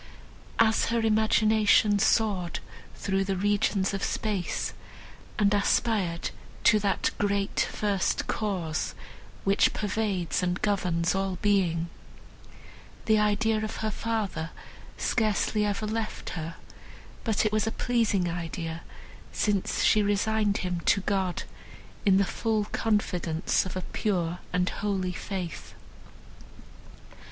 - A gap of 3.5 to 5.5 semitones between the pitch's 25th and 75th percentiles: No, average, 3.0 semitones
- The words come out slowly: Yes, slow, 115 wpm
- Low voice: No, high, 200 Hz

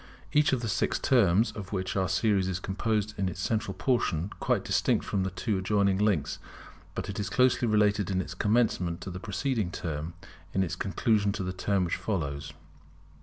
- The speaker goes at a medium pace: Yes, average, 195 wpm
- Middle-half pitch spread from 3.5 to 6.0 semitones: No, average, 2.7 semitones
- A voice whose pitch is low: Yes, low, 100 Hz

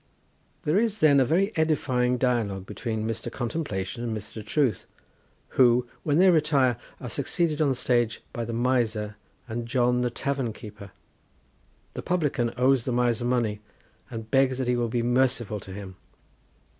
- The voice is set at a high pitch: No, low, 125 Hz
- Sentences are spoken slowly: No, average, 160 wpm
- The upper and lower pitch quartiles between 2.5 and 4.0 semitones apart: Yes, average, 3.2 semitones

